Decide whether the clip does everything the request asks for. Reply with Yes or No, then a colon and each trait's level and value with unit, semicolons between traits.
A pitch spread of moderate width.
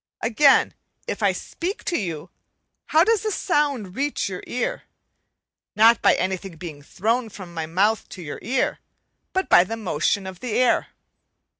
No: wide, 6.8 semitones